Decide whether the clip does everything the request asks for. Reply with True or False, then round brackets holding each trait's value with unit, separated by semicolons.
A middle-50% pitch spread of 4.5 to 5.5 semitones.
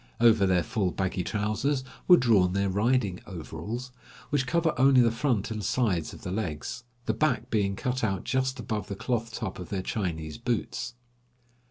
True (4.8 semitones)